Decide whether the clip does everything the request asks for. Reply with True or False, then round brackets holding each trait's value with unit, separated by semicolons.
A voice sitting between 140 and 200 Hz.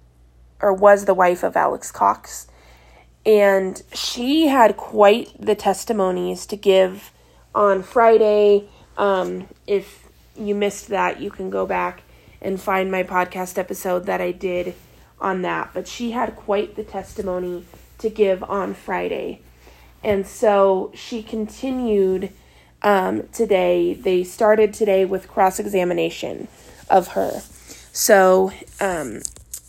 True (190 Hz)